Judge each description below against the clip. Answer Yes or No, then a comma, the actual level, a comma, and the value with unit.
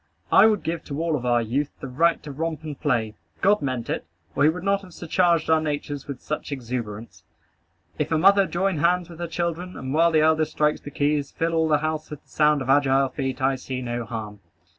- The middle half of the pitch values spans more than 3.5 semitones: Yes, average, 3.9 semitones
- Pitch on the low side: No, medium, 150 Hz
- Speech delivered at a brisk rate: Yes, fast, 230 wpm